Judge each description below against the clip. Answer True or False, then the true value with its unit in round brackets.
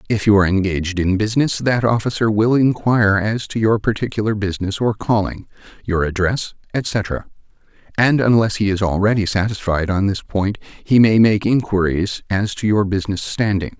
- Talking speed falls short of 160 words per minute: False (165 wpm)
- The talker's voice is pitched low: True (105 Hz)